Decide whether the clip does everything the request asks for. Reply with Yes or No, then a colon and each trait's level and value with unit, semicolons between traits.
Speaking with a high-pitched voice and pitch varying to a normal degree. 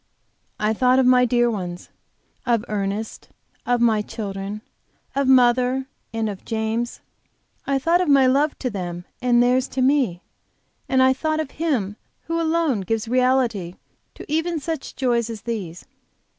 Yes: high, 245 Hz; average, 3.9 semitones